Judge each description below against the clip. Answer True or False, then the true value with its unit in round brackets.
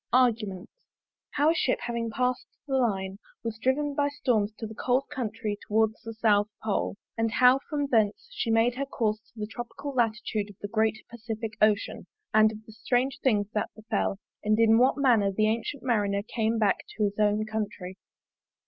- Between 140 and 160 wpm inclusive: False (185 wpm)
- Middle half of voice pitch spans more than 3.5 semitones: False (2.8 semitones)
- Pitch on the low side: False (220 Hz)